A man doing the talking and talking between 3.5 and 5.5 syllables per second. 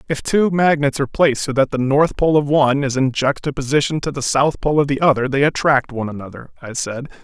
No: male; 6.0 syllables/s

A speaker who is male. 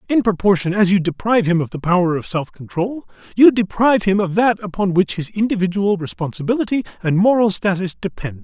Yes: male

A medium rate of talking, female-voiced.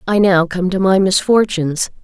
Yes: average, 175 wpm; female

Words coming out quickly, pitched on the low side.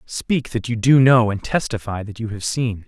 Yes: fast, 230 wpm; low, 115 Hz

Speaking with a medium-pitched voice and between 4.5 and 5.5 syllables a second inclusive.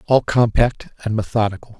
No: low, 110 Hz; 5.4 syllables/s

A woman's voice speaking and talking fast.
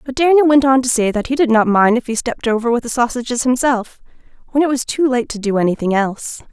Yes: female; fast, 260 wpm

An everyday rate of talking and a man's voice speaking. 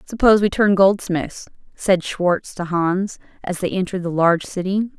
No: average, 170 wpm; female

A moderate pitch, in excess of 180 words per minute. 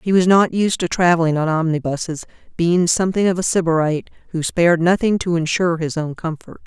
Yes: medium, 170 Hz; average, 190 wpm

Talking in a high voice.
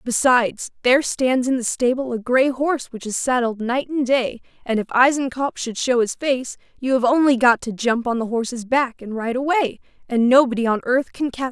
Yes: very high, 250 Hz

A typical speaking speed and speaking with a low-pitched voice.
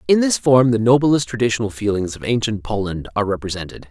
Yes: average, 185 wpm; low, 115 Hz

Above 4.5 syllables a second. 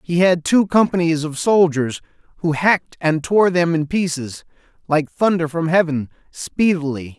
No: 4.4 syllables/s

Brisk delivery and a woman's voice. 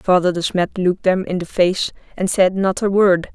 Yes: fast, 235 wpm; female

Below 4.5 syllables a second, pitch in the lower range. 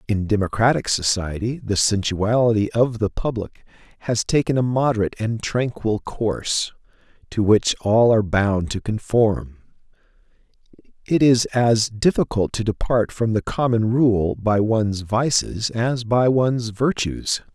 Yes: 4.3 syllables/s; low, 110 Hz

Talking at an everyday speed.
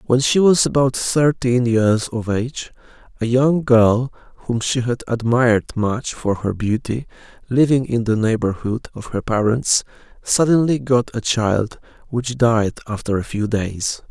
Yes: average, 155 wpm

